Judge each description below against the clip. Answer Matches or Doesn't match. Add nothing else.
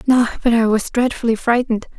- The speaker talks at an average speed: Matches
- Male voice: Doesn't match